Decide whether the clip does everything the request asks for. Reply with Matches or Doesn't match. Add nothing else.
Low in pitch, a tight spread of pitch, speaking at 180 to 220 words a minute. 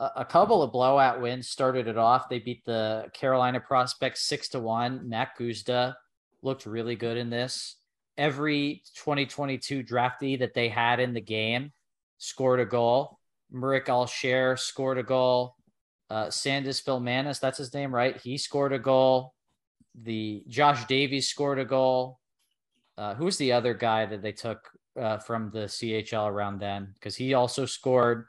Doesn't match